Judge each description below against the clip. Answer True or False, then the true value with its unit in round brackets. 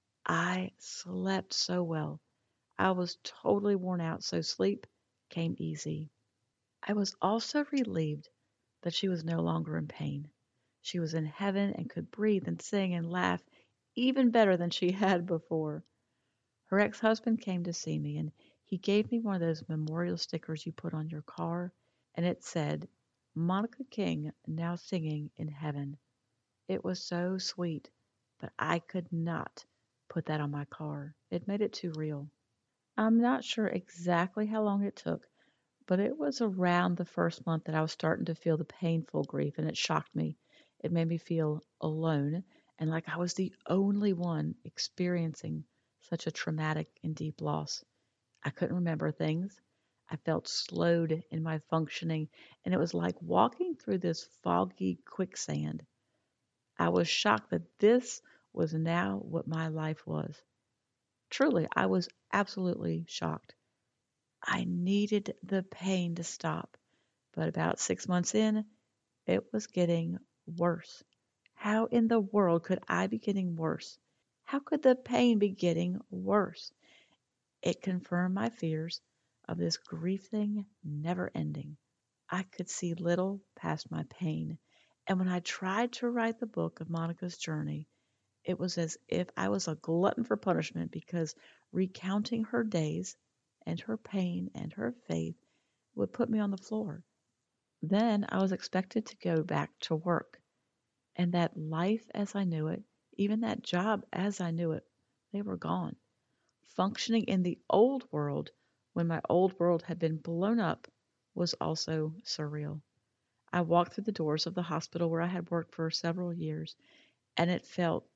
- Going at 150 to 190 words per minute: True (160 wpm)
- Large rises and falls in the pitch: False (4.1 semitones)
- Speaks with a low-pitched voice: False (170 Hz)